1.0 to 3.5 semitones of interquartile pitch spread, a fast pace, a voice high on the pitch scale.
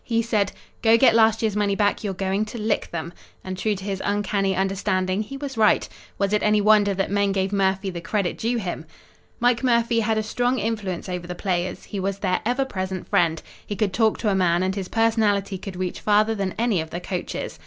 Yes: average, 2.7 semitones; fast, 225 wpm; high, 200 Hz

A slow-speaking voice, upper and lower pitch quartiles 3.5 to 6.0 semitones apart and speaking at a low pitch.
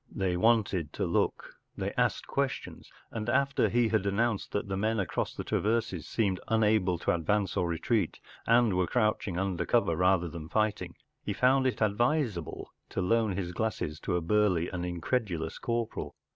No: average, 170 wpm; average, 4.2 semitones; low, 100 Hz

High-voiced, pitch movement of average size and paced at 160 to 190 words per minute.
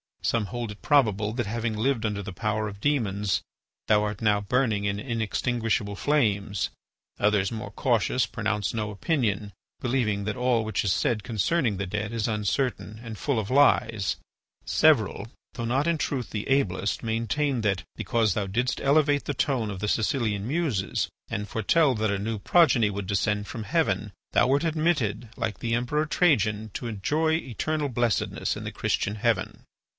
No: low, 110 Hz; average, 3.9 semitones; average, 170 wpm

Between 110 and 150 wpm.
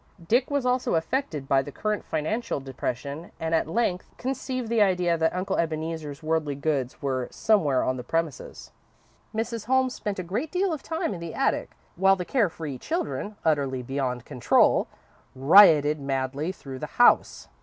No: average, 165 wpm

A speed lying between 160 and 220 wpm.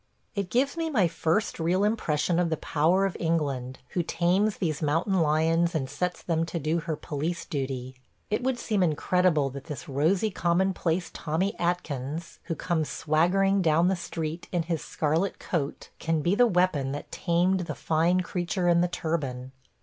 Yes: average, 175 wpm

